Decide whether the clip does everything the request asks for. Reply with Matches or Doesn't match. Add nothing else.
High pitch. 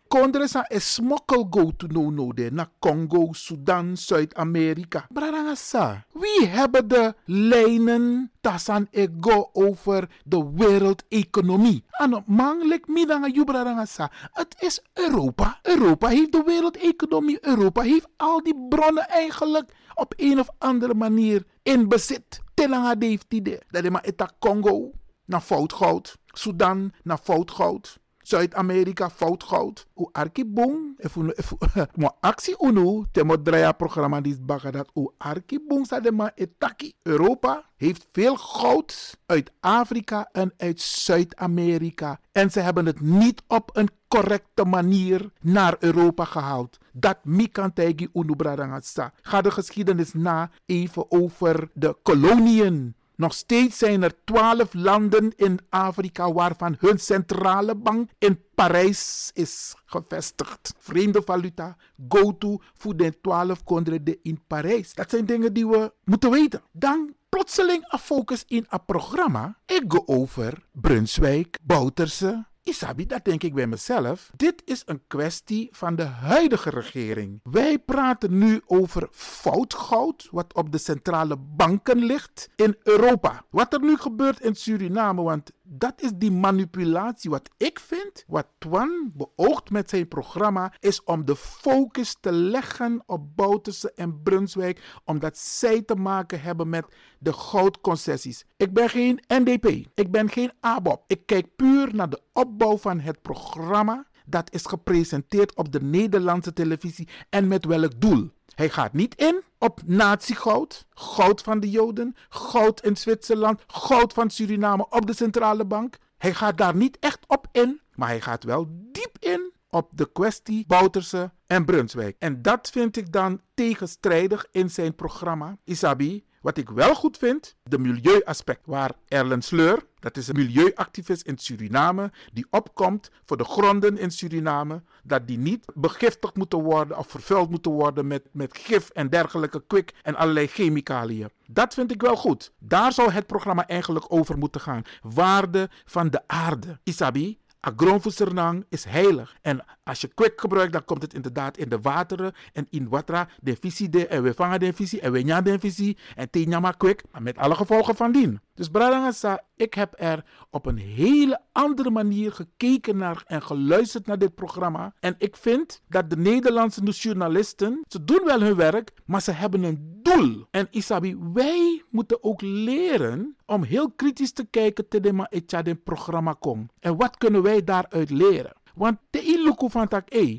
Matches